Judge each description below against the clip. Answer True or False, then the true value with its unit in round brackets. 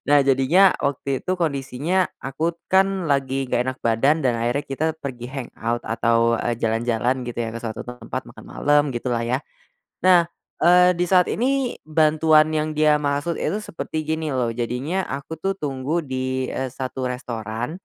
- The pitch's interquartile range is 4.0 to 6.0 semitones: True (4.6 semitones)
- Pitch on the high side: False (140 Hz)